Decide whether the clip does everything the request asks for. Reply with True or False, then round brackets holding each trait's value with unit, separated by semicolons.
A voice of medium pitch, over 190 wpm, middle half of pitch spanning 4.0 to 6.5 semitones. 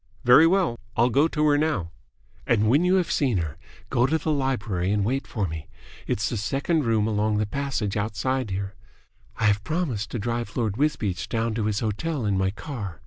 False (115 Hz; 200 wpm; 5.3 semitones)